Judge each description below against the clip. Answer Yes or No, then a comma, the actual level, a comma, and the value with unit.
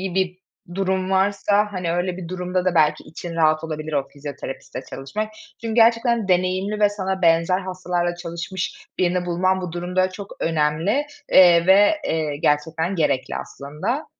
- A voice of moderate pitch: Yes, medium, 180 Hz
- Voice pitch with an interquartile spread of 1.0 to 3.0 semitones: Yes, narrow, 2.6 semitones